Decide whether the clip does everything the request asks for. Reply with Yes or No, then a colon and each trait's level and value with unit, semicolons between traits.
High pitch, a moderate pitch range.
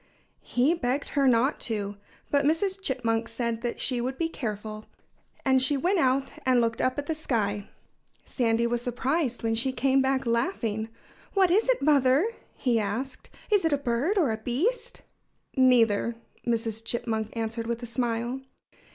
Yes: very high, 250 Hz; average, 3.6 semitones